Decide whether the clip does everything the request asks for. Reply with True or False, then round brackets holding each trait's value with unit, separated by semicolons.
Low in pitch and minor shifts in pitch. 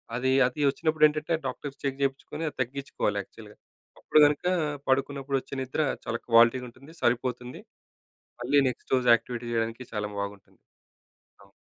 False (130 Hz; 3.0 semitones)